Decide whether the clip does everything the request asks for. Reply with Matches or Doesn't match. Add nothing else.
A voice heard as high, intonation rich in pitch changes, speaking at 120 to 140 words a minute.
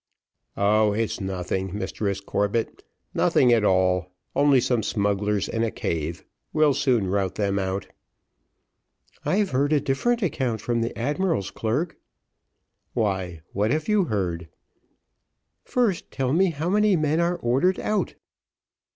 Doesn't match